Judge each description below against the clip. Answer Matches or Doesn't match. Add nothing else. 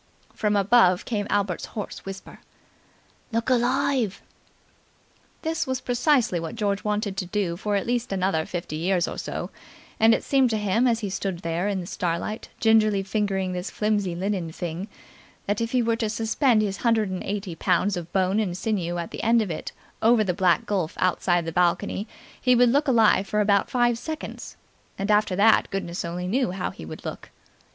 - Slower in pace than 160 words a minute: Doesn't match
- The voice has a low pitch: Doesn't match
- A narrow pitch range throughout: Doesn't match